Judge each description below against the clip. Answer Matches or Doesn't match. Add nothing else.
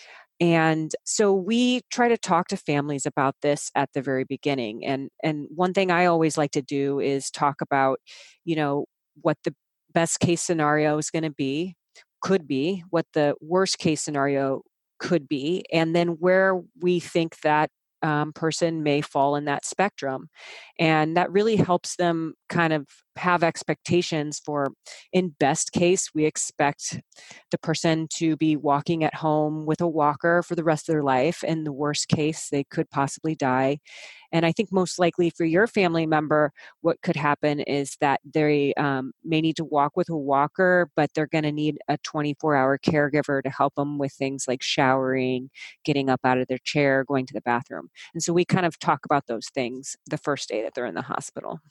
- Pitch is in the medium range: Matches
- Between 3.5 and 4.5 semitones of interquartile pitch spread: Doesn't match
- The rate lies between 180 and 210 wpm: Matches